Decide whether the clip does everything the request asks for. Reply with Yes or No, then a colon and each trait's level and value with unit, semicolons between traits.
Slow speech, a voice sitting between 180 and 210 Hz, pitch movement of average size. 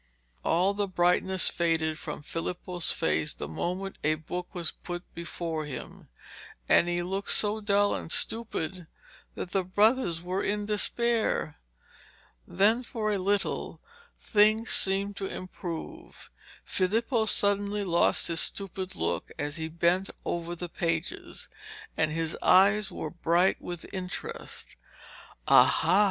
Yes: slow, 130 wpm; medium, 185 Hz; average, 3.3 semitones